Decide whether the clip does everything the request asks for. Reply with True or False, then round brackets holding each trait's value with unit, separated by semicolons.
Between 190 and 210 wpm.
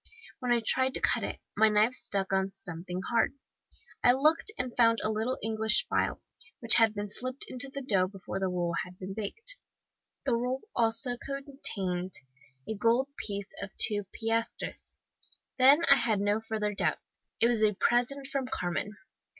False (170 wpm)